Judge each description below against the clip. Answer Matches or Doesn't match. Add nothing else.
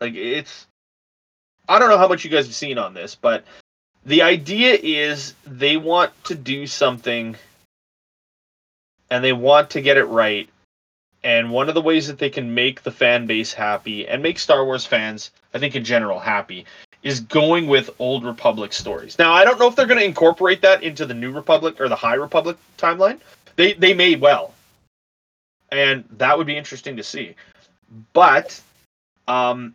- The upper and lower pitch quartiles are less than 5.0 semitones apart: Doesn't match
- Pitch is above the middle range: Doesn't match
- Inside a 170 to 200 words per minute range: Matches